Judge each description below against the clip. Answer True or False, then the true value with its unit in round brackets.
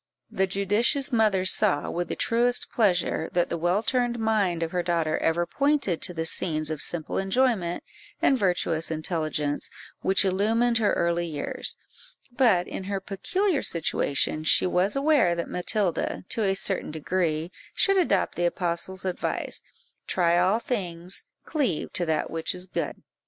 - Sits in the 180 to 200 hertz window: True (185 Hz)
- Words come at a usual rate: True (155 wpm)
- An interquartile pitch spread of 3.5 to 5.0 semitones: True (4.5 semitones)